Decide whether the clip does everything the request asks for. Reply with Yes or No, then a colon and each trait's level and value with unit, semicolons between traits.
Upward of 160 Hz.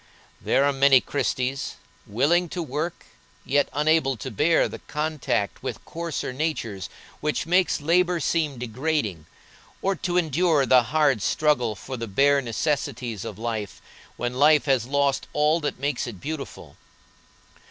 No: medium, 140 Hz